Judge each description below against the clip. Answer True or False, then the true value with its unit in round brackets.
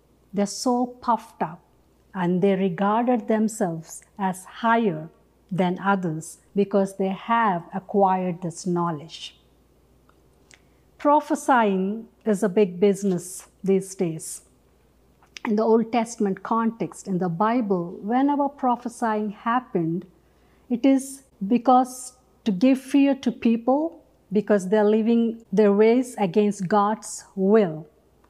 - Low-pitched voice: False (210 Hz)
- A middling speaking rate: False (110 wpm)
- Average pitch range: True (3.6 semitones)